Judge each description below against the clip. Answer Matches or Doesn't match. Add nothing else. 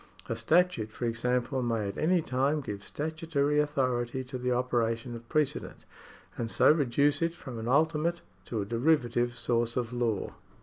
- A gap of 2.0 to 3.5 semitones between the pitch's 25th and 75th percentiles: Doesn't match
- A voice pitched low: Matches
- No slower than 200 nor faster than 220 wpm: Doesn't match